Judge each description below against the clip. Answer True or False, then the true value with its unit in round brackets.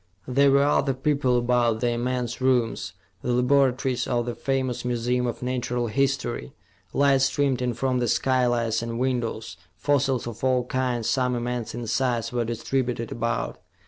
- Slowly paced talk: False (155 wpm)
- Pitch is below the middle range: True (125 Hz)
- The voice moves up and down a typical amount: False (1.8 semitones)